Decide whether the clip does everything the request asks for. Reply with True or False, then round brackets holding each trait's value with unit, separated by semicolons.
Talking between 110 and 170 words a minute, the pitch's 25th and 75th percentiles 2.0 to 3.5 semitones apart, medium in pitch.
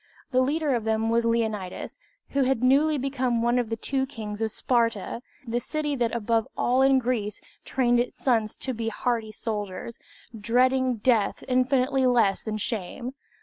False (165 wpm; 2.7 semitones; 240 Hz)